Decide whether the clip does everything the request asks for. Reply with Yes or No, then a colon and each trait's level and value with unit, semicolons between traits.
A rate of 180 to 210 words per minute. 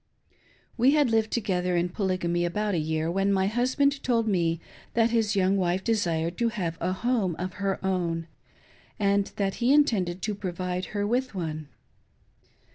No: average, 165 wpm